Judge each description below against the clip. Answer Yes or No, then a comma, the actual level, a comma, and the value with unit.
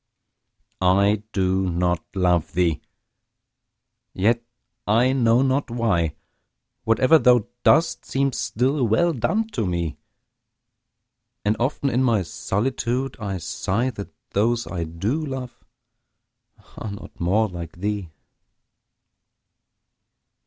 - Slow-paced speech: Yes, slow, 105 wpm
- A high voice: No, low, 110 Hz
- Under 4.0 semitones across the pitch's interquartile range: No, wide, 5.6 semitones